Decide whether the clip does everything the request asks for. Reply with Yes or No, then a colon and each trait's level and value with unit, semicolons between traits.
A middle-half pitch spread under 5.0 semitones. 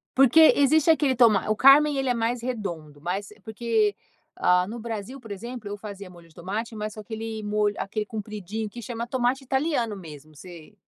Yes: average, 3.5 semitones